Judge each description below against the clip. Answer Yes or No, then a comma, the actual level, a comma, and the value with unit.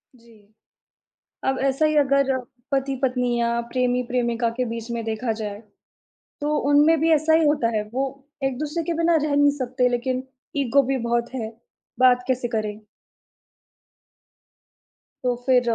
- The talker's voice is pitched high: Yes, very high, 255 Hz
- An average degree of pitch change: Yes, average, 3.1 semitones